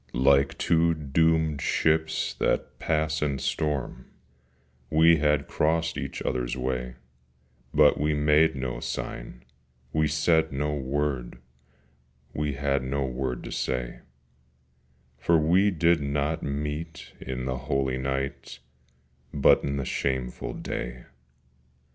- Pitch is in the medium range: No, very low, 75 Hz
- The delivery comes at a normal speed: No, slow, 120 wpm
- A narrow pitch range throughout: No, average, 3.0 semitones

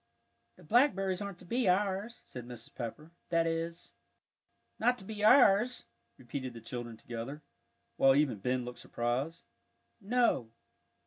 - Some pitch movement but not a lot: No, wide, 8.6 semitones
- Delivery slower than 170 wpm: Yes, average, 140 wpm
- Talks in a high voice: No, medium, 165 Hz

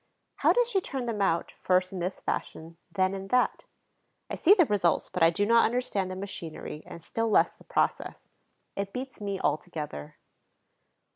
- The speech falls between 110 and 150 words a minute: No, average, 175 wpm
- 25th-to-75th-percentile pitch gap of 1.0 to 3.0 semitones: No, average, 5.0 semitones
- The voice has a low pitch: No, high, 195 Hz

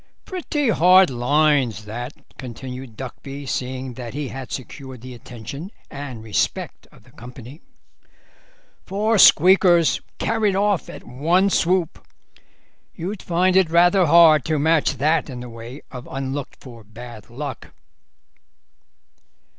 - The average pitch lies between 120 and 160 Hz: Yes, medium, 140 Hz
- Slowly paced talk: Yes, slow, 125 wpm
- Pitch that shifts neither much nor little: No, wide, 5.8 semitones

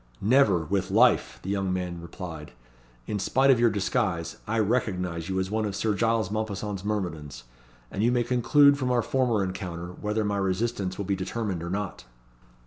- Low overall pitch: Yes, low, 100 Hz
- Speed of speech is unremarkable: Yes, average, 180 wpm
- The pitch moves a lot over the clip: No, average, 3.4 semitones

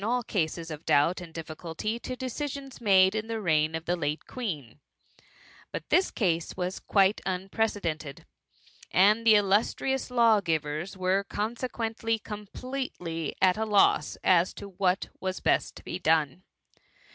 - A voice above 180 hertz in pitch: Yes, high, 190 Hz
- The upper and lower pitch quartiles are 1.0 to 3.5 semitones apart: No, average, 5.2 semitones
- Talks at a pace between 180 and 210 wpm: No, average, 145 wpm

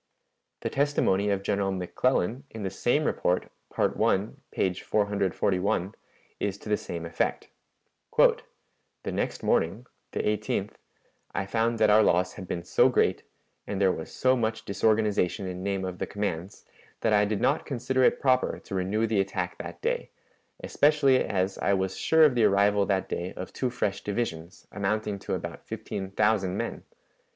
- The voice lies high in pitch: No, low, 100 Hz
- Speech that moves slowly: No, average, 165 wpm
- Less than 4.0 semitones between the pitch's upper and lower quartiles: Yes, average, 2.8 semitones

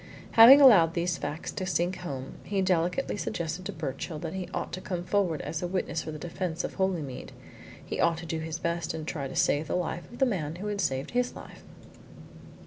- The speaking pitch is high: No, medium, 175 Hz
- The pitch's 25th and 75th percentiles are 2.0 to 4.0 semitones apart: Yes, average, 3.0 semitones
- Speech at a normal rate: No, fast, 220 wpm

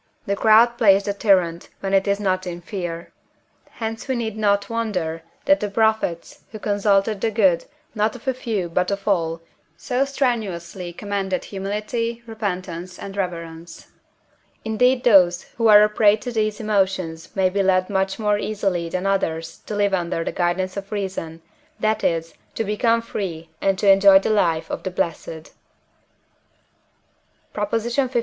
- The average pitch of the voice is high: Yes, high, 200 Hz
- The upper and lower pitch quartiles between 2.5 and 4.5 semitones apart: Yes, average, 3.3 semitones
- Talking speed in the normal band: Yes, average, 160 wpm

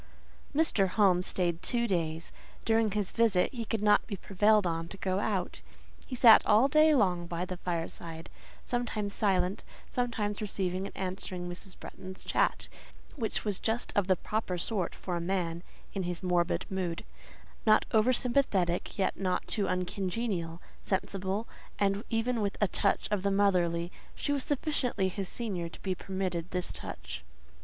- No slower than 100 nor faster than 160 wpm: Yes, average, 155 wpm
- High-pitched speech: Yes, high, 195 Hz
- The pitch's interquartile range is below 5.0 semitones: Yes, average, 3.4 semitones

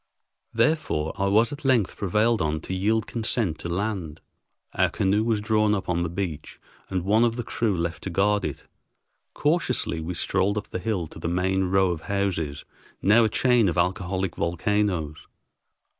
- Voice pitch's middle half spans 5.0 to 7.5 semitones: No, average, 4.0 semitones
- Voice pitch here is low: Yes, very low, 95 Hz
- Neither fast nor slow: Yes, average, 175 wpm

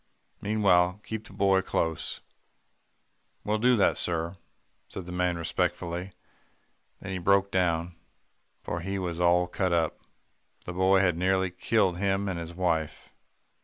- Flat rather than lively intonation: Yes, narrow, 2.1 semitones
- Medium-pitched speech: No, very low, 90 Hz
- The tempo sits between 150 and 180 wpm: No, average, 140 wpm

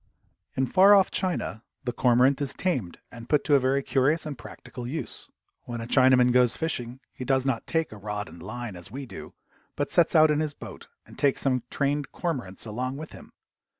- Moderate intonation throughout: Yes, average, 3.7 semitones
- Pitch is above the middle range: No, low, 130 Hz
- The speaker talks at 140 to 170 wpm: No, fast, 205 wpm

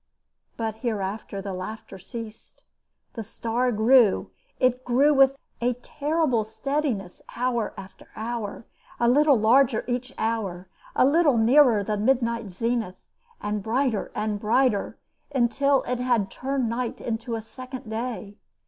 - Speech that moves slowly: Yes, slow, 130 wpm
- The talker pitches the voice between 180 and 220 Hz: No, high, 235 Hz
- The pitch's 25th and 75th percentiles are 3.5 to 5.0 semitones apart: No, average, 3.0 semitones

